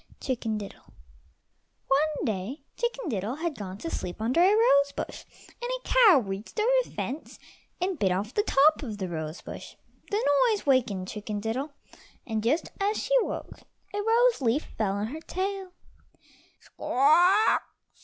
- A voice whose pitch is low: No, very high, 275 Hz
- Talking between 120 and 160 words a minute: Yes, average, 155 wpm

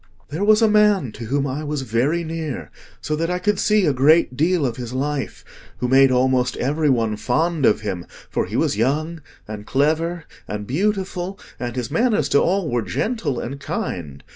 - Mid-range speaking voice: Yes, medium, 145 Hz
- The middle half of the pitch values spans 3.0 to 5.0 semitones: No, wide, 5.5 semitones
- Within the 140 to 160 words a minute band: No, average, 190 wpm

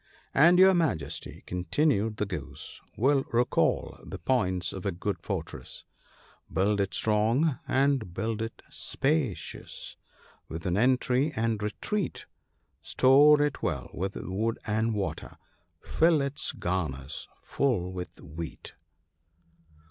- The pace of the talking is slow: Yes, slow, 125 wpm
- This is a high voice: No, low, 110 Hz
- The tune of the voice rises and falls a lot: Yes, wide, 6.8 semitones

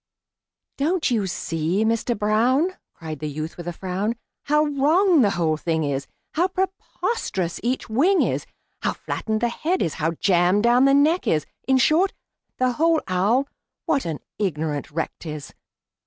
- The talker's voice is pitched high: Yes, high, 220 Hz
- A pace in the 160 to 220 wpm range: Yes, average, 165 wpm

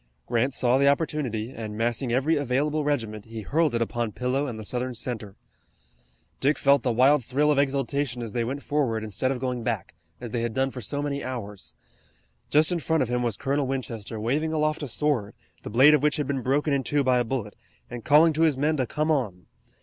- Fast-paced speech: Yes, fast, 220 wpm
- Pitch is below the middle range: Yes, low, 130 Hz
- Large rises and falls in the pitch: No, average, 3.7 semitones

